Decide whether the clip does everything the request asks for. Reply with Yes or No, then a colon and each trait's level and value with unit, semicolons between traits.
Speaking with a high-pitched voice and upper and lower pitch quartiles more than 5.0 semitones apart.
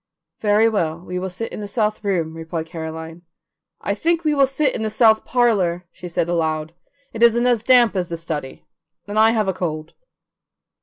Yes: high, 200 Hz; wide, 5.4 semitones